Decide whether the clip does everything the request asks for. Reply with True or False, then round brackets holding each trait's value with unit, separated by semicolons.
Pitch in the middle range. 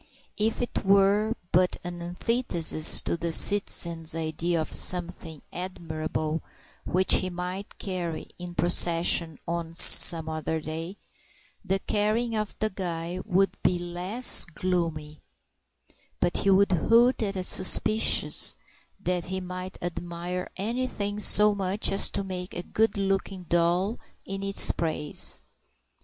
True (180 Hz)